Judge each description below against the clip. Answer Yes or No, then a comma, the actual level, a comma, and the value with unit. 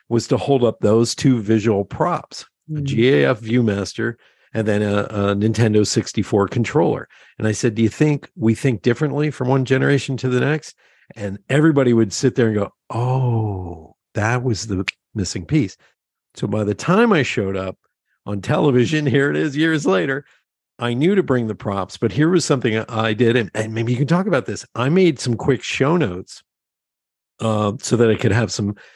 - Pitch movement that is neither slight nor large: Yes, average, 4.2 semitones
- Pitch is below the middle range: Yes, low, 120 Hz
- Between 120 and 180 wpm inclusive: No, average, 195 wpm